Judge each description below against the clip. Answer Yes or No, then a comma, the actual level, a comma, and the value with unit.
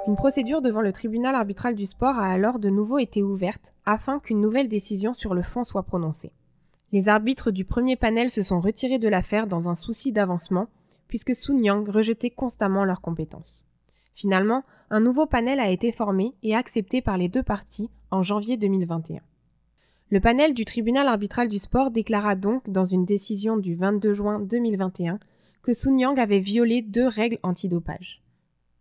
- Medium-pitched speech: No, high, 210 Hz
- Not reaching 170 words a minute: No, average, 175 wpm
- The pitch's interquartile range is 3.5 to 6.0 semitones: Yes, average, 4.0 semitones